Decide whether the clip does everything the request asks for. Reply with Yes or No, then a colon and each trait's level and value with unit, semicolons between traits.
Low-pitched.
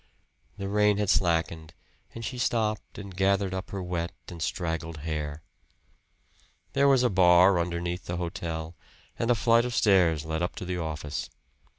Yes: very low, 90 Hz